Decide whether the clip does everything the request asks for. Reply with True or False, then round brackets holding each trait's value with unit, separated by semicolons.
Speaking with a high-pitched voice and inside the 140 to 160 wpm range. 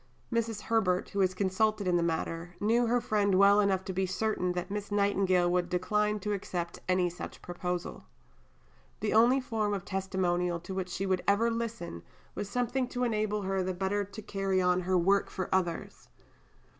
False (195 Hz; 180 wpm)